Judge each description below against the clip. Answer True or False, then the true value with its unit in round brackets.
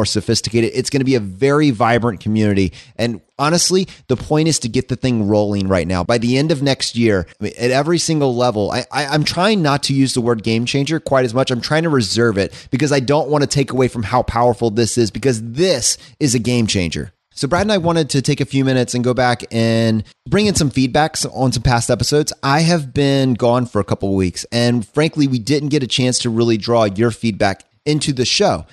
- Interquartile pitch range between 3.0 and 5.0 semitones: True (3.8 semitones)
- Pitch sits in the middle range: False (125 Hz)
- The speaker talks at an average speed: False (235 wpm)